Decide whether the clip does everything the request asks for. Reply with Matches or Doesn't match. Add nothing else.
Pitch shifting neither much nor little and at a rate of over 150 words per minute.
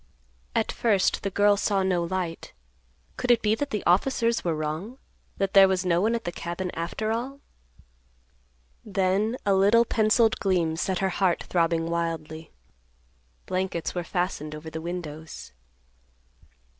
Doesn't match